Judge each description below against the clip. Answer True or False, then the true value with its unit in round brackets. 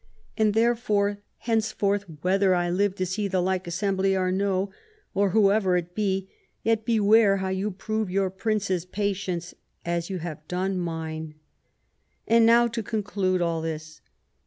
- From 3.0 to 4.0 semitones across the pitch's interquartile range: False (2.6 semitones)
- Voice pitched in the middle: False (195 Hz)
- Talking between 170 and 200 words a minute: False (155 wpm)